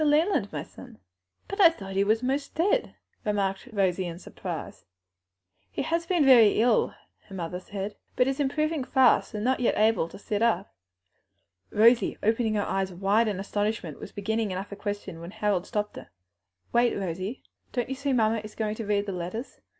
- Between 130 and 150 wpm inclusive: No, average, 180 wpm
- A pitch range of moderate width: Yes, average, 4.3 semitones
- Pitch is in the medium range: No, high, 215 Hz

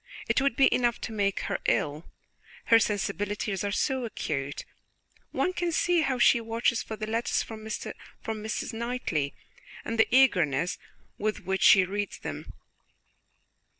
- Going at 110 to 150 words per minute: Yes, average, 145 wpm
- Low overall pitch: No, high, 220 Hz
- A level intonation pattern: No, average, 3.4 semitones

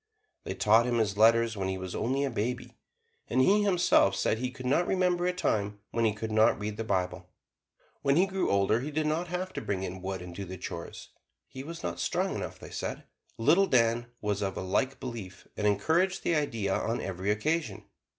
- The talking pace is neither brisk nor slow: No, fast, 220 wpm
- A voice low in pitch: Yes, low, 115 Hz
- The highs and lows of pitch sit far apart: Yes, wide, 6.8 semitones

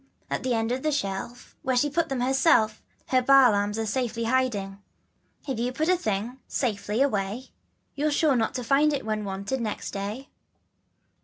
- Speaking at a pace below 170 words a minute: No, average, 185 wpm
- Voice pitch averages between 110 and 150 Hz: No, high, 245 Hz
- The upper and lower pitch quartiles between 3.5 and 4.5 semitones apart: Yes, average, 4.0 semitones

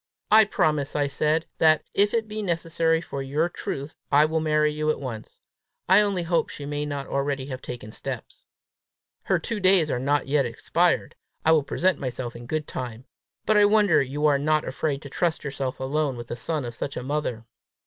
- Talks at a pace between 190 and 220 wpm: Yes, average, 200 wpm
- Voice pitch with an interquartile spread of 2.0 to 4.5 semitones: Yes, average, 3.4 semitones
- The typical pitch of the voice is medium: Yes, medium, 150 Hz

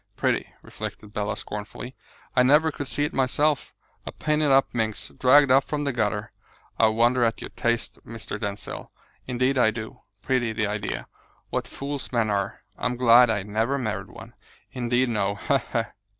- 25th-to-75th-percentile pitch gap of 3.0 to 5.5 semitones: Yes, average, 3.6 semitones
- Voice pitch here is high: No, low, 120 Hz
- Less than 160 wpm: No, average, 170 wpm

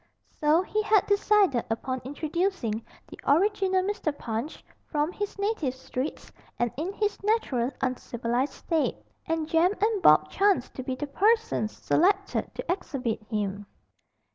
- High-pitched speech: Yes, very high, 315 Hz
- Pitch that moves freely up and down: Yes, wide, 7.8 semitones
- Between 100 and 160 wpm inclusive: Yes, average, 140 wpm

